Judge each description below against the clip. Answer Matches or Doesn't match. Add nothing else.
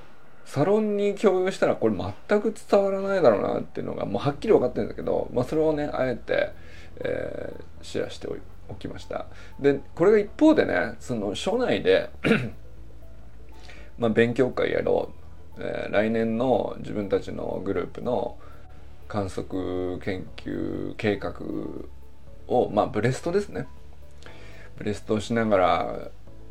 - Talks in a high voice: Doesn't match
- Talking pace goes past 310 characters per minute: Doesn't match